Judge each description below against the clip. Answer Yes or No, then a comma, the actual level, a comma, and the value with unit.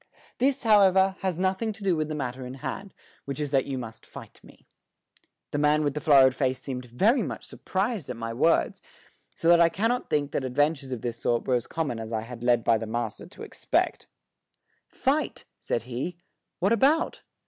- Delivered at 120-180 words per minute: No, fast, 205 wpm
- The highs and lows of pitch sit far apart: Yes, wide, 7.2 semitones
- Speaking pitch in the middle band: Yes, medium, 145 Hz